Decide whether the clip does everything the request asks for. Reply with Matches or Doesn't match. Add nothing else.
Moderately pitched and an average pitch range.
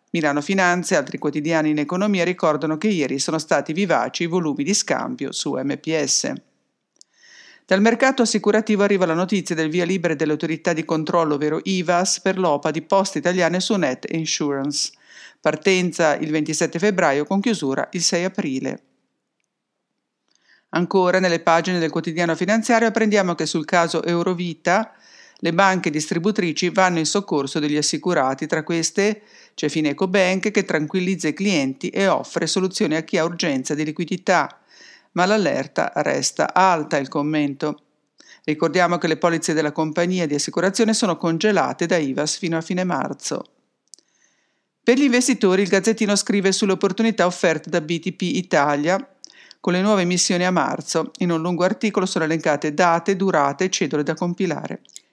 Matches